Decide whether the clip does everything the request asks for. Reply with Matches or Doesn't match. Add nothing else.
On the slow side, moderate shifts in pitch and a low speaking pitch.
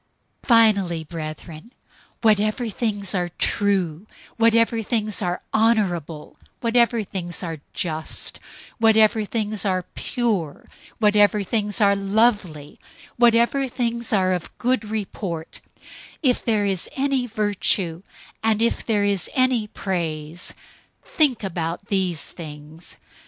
Doesn't match